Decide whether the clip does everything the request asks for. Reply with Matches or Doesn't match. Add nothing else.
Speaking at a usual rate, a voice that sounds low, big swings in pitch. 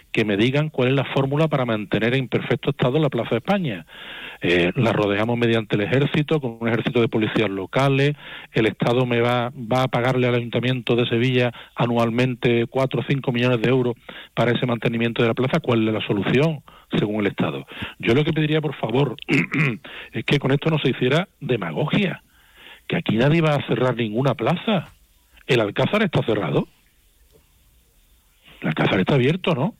Doesn't match